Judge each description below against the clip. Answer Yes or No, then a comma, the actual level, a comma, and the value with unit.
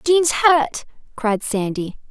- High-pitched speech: Yes, very high, 265 Hz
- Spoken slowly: Yes, slow, 115 wpm